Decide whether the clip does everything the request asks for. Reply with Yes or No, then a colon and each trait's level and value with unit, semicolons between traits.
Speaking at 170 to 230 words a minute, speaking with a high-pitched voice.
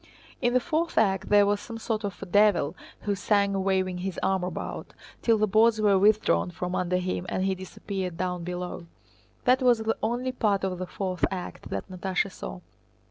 Yes: average, 190 wpm; high, 195 Hz